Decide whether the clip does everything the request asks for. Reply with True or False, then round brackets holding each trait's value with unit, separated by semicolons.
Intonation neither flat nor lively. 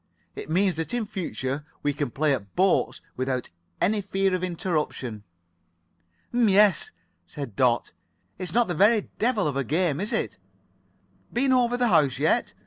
False (6.9 semitones)